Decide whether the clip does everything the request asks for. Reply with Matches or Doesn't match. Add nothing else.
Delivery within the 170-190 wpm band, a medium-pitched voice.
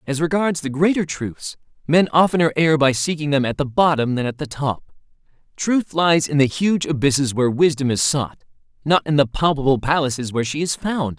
Doesn't match